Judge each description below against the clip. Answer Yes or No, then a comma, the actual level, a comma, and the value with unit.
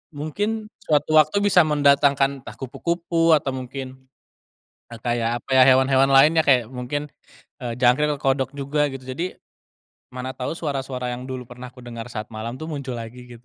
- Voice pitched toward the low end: Yes, low, 130 Hz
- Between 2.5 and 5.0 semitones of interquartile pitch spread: Yes, average, 2.9 semitones